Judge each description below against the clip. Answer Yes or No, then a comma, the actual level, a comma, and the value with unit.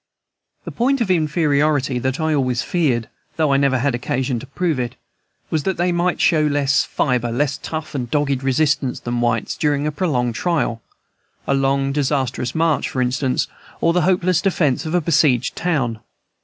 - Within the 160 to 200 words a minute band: Yes, average, 175 wpm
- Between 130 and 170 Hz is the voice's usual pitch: Yes, medium, 140 Hz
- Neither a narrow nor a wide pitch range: Yes, average, 3.9 semitones